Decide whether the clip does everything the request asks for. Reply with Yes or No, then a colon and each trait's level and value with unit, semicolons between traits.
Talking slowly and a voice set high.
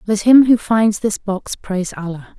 No: average, 200 wpm; high, 205 Hz